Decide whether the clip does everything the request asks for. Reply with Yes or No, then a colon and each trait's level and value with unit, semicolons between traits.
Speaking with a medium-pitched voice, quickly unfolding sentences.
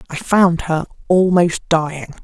No: medium, 170 Hz; slow, 135 wpm